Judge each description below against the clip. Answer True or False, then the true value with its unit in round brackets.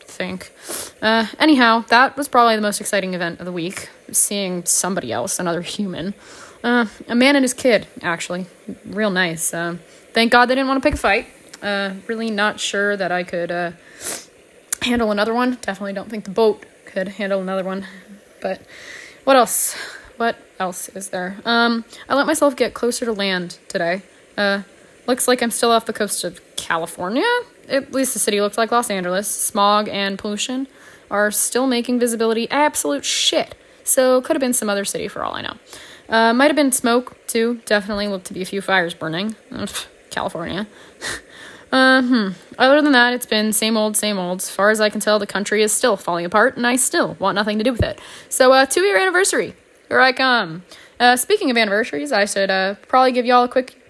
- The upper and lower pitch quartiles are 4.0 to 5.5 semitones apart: True (4.3 semitones)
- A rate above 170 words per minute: True (200 wpm)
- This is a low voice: False (220 Hz)